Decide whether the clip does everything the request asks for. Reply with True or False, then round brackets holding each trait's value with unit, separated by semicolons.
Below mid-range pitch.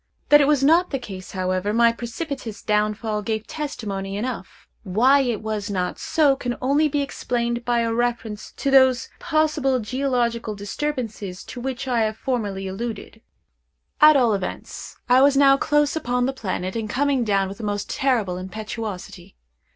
False (235 Hz)